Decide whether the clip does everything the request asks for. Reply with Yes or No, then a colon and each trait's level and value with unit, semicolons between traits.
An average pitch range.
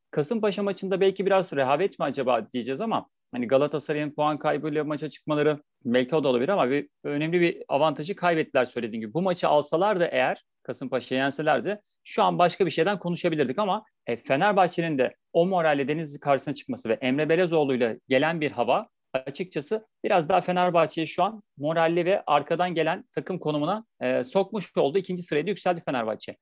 Yes: average, 4.1 semitones